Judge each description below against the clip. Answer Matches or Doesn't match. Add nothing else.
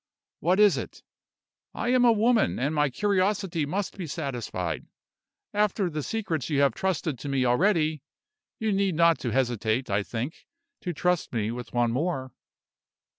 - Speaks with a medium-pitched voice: Matches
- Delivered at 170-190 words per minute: Doesn't match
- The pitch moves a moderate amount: Doesn't match